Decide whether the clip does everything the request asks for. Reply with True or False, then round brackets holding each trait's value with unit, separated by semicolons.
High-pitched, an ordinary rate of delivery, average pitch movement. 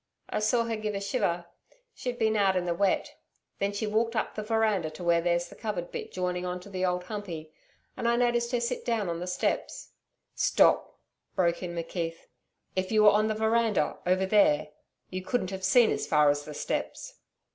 False (195 Hz; 210 wpm; 4.0 semitones)